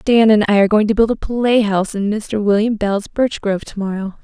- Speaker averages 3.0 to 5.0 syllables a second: No, 5.9 syllables/s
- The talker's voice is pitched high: Yes, high, 210 Hz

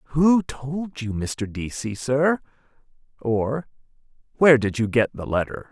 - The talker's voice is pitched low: Yes, low, 130 Hz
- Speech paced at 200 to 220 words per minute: No, slow, 135 wpm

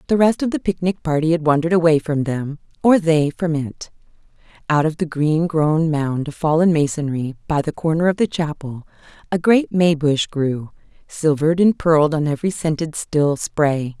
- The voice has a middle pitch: Yes, medium, 160 Hz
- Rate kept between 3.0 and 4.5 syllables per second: No, 5.0 syllables/s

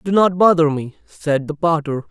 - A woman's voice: No, male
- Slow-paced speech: No, average, 200 wpm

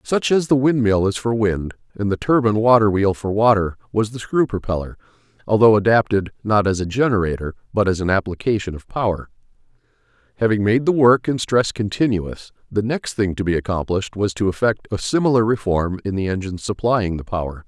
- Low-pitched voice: Yes, low, 105 Hz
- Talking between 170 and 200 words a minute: Yes, average, 185 wpm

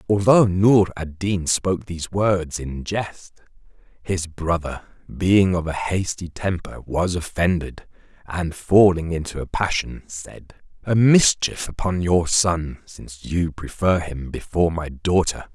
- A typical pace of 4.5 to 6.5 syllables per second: No, 4.0 syllables/s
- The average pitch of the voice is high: No, very low, 90 Hz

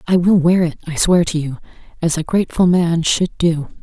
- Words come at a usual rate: No, fast, 220 wpm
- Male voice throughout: No, female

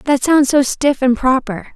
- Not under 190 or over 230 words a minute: Yes, fast, 205 wpm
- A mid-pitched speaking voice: No, very high, 265 Hz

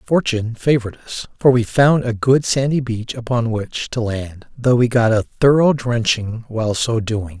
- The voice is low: Yes, low, 120 Hz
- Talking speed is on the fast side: No, average, 185 wpm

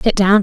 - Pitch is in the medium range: No, high, 200 Hz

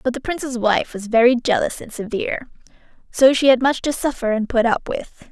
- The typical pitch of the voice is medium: No, high, 245 Hz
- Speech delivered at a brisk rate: Yes, fast, 215 wpm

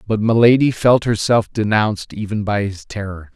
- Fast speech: No, average, 160 wpm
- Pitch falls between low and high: No, low, 105 Hz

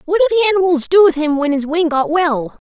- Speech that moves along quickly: Yes, fast, 270 wpm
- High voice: Yes, very high, 325 Hz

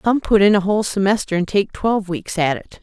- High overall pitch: Yes, high, 195 Hz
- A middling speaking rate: No, fast, 255 wpm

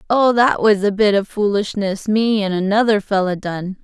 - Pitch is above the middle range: Yes, high, 205 Hz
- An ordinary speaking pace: Yes, average, 190 wpm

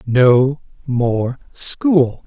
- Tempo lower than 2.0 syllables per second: Yes, 1.7 syllables/s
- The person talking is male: Yes, male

